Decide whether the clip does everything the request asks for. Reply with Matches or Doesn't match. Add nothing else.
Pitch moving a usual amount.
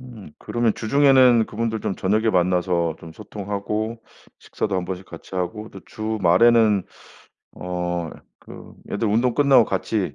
Matches